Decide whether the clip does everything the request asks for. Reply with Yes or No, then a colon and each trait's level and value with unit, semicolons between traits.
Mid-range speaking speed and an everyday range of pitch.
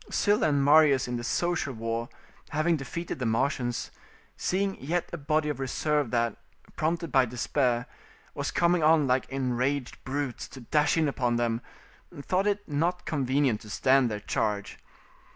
Yes: average, 155 wpm; average, 4.3 semitones